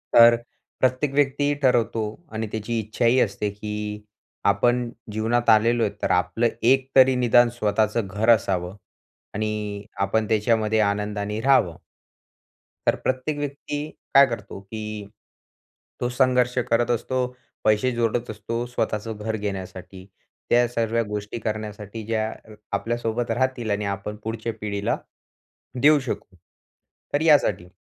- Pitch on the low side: Yes, low, 110 Hz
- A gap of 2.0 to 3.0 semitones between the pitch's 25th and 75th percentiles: Yes, average, 2.7 semitones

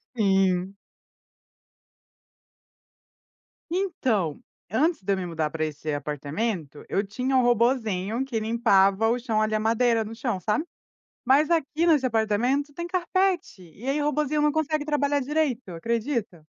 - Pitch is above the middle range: Yes, high, 230 Hz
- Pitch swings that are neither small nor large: No, wide, 6.9 semitones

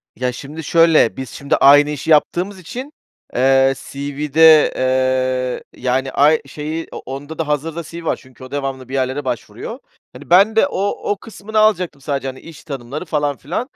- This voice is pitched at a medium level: Yes, medium, 145 Hz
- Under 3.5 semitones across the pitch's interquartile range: No, average, 3.8 semitones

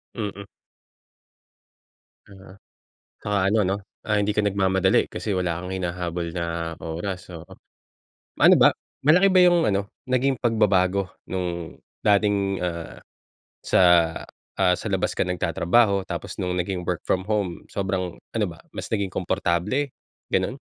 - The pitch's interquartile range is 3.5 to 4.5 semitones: No, average, 2.7 semitones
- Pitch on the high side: No, very low, 95 Hz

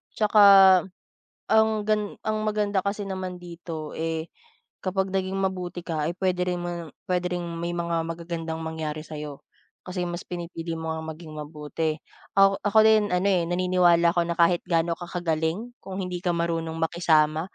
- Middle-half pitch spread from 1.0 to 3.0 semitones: Yes, narrow, 2.4 semitones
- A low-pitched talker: No, medium, 175 Hz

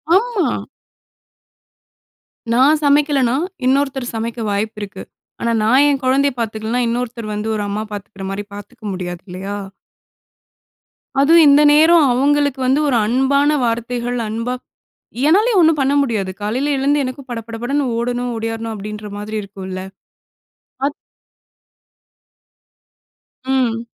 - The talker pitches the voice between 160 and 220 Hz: No, high, 245 Hz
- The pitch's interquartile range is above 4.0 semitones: Yes, average, 4.7 semitones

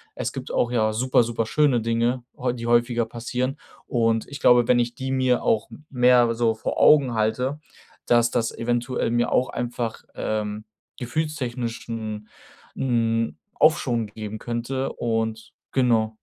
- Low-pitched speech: Yes, low, 120 Hz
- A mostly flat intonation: Yes, narrow, 1.9 semitones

